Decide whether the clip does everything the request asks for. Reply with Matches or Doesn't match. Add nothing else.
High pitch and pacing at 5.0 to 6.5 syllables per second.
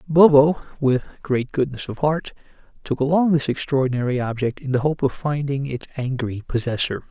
Doesn't match